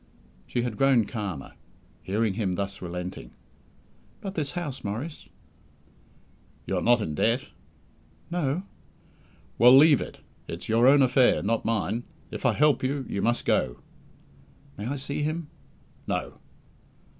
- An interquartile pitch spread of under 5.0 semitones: No, wide, 5.5 semitones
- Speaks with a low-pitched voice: Yes, low, 120 Hz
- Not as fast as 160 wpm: Yes, slow, 135 wpm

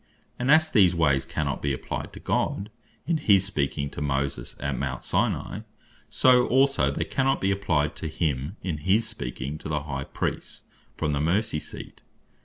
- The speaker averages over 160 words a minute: Yes, average, 175 wpm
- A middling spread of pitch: No, wide, 7.0 semitones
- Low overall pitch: Yes, very low, 80 Hz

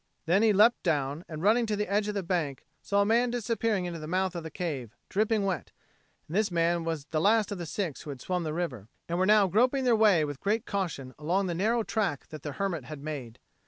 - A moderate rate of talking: No, fast, 245 wpm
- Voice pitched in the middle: Yes, medium, 180 Hz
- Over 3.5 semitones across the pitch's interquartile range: Yes, average, 5.2 semitones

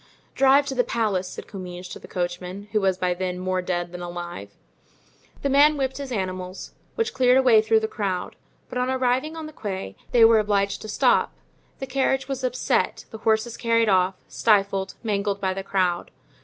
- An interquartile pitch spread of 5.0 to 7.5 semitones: Yes, average, 5.3 semitones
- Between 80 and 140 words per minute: No, average, 195 wpm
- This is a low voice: No, high, 210 Hz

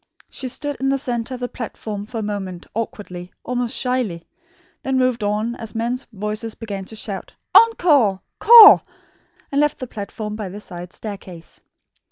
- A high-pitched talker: Yes, high, 225 Hz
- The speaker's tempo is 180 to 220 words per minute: No, average, 165 wpm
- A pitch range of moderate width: Yes, average, 3.8 semitones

